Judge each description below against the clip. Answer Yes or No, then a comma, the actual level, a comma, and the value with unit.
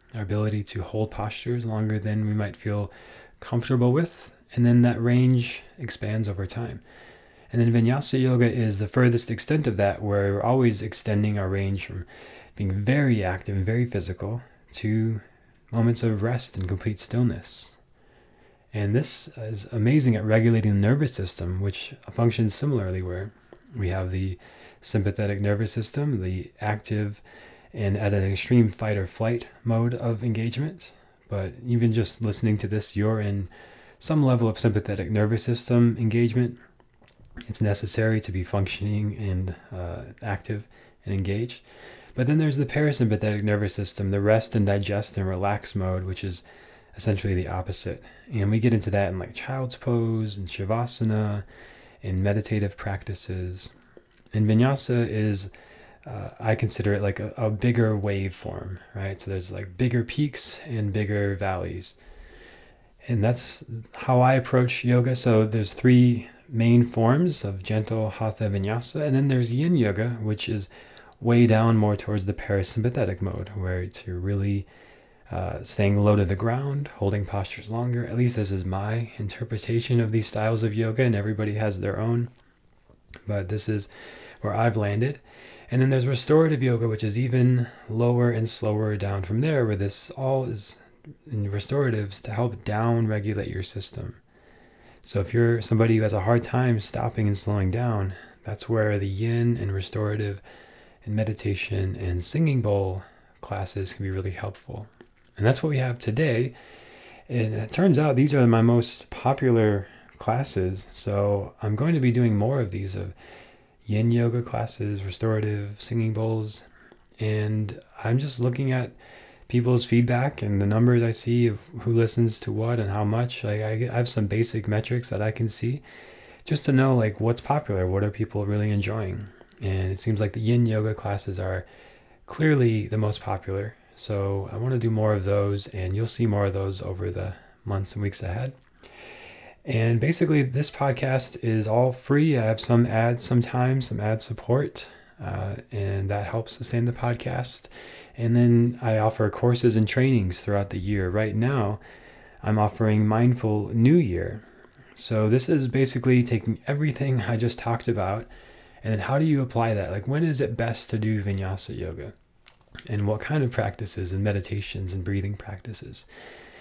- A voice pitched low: Yes, low, 110 Hz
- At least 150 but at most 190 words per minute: Yes, average, 165 wpm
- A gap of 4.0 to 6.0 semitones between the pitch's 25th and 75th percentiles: No, average, 3.0 semitones